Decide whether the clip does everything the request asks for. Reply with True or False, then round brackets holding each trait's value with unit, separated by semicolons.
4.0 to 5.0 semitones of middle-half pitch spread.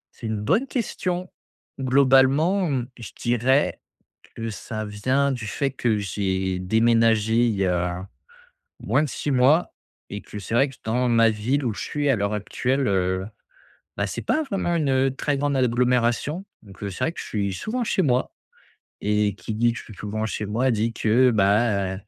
True (4.5 semitones)